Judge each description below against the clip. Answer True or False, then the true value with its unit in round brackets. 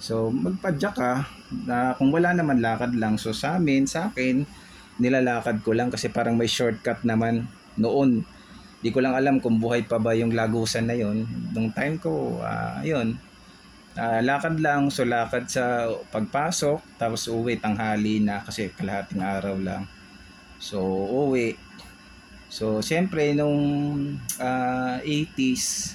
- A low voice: True (120 Hz)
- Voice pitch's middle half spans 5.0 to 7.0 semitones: False (3.8 semitones)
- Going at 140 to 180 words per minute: True (145 wpm)